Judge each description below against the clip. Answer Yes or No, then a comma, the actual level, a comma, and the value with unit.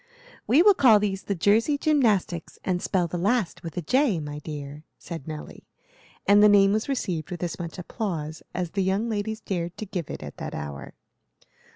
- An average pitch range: Yes, average, 4.7 semitones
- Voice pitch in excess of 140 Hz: Yes, high, 190 Hz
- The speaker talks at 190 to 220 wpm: Yes, average, 195 wpm